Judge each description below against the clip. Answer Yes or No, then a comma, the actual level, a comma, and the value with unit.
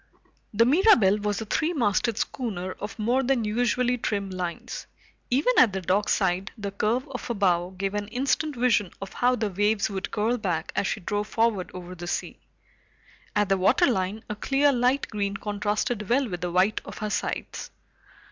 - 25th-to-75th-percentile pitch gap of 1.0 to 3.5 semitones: No, average, 4.0 semitones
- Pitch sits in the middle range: No, high, 210 Hz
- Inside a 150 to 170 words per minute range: No, average, 180 wpm